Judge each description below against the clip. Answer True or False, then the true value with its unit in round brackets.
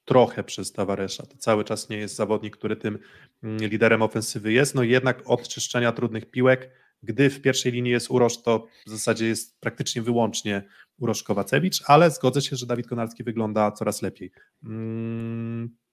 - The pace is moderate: False (165 wpm)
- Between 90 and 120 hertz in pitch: True (115 Hz)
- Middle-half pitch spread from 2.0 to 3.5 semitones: True (2.4 semitones)